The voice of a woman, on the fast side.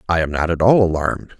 No: male; fast, 260 wpm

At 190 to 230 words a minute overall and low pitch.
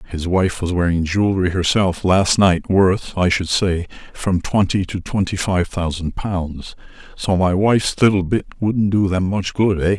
No: average, 180 wpm; very low, 95 Hz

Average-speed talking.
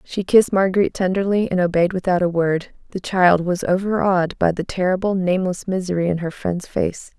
Yes: average, 185 wpm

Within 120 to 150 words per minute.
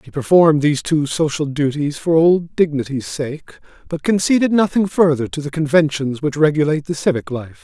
No: average, 175 wpm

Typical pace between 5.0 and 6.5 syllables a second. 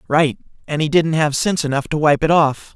Yes: 5.7 syllables/s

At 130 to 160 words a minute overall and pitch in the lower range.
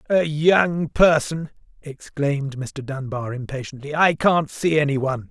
No: slow, 135 wpm; medium, 145 Hz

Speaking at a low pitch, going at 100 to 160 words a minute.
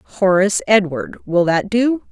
No: high, 200 Hz; average, 140 wpm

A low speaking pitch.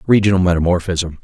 Yes: very low, 90 Hz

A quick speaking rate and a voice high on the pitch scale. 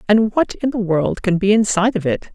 Yes: fast, 255 wpm; high, 205 Hz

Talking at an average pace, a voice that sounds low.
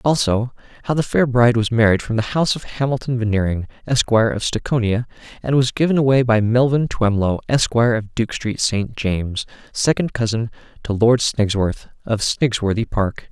Yes: average, 165 wpm; low, 115 Hz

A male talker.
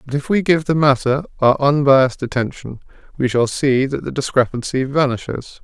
Yes: male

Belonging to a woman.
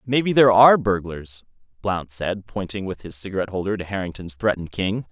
No: male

